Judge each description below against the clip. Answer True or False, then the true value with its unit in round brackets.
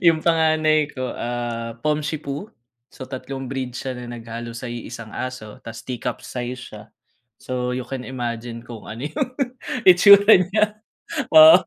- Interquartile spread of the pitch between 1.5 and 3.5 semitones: False (4.6 semitones)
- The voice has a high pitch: False (130 Hz)